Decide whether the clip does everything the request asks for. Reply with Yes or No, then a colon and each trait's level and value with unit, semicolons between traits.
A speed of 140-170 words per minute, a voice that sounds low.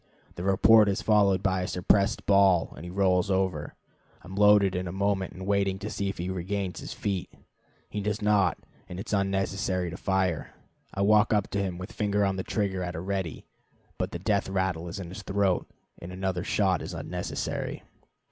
No: average, 200 wpm; very low, 95 Hz